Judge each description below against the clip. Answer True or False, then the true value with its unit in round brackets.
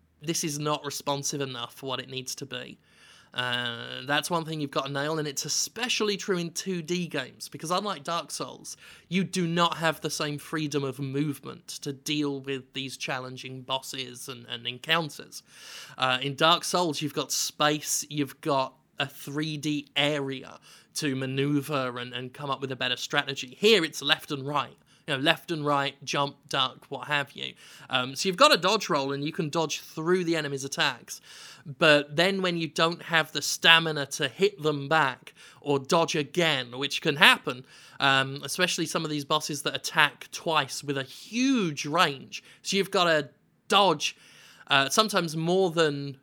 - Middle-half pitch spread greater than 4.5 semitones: False (3.2 semitones)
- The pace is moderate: True (180 wpm)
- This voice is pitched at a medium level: True (150 Hz)